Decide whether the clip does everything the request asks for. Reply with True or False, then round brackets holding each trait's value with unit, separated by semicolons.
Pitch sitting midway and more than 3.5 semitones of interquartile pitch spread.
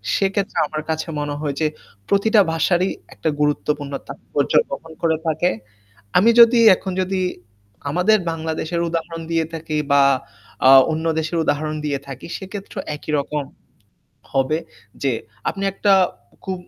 True (160 Hz; 4.0 semitones)